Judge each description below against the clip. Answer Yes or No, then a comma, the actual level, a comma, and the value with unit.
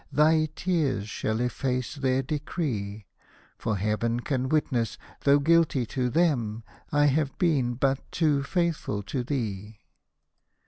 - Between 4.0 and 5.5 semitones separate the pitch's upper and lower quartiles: Yes, average, 4.6 semitones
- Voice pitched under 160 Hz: Yes, low, 135 Hz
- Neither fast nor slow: No, slow, 125 wpm